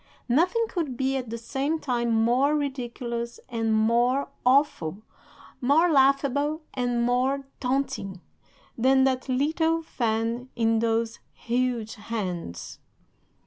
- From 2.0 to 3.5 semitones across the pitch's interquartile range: Yes, average, 3.2 semitones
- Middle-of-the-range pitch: No, very high, 250 Hz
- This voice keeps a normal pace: No, slow, 110 wpm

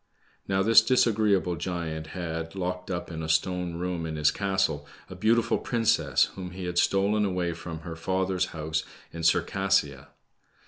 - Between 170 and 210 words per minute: No, average, 155 wpm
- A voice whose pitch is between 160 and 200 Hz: No, very low, 90 Hz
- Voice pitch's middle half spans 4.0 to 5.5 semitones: No, average, 3.0 semitones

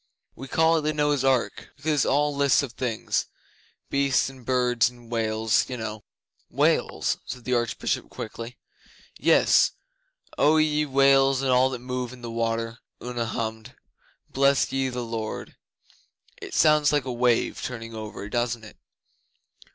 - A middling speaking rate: Yes, average, 150 wpm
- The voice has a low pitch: Yes, low, 125 Hz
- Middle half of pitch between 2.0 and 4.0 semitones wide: Yes, average, 3.1 semitones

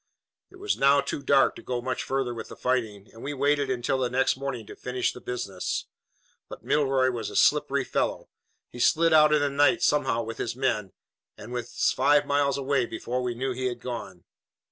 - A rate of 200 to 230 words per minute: Yes, fast, 205 wpm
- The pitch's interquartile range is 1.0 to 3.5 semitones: Yes, average, 2.7 semitones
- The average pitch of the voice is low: Yes, low, 130 Hz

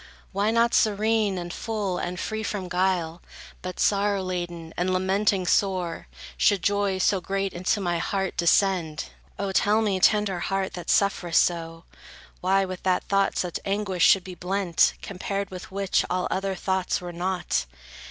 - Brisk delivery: No, average, 160 wpm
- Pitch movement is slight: Yes, narrow, 2.0 semitones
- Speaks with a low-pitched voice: No, high, 190 Hz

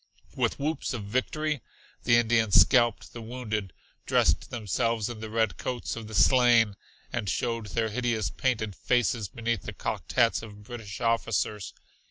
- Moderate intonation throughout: No, narrow, 2.1 semitones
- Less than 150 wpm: No, average, 155 wpm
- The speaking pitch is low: Yes, low, 115 Hz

